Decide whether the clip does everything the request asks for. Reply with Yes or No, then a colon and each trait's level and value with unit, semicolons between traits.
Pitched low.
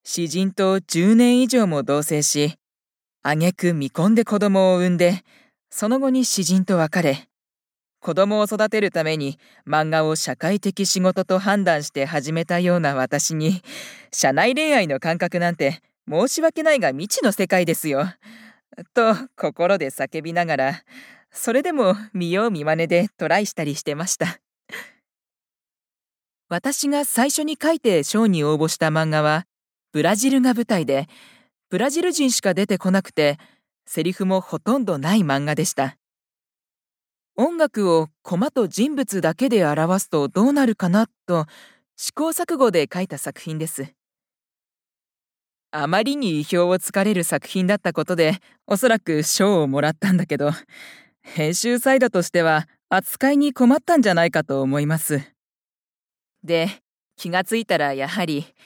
No: medium, 185 Hz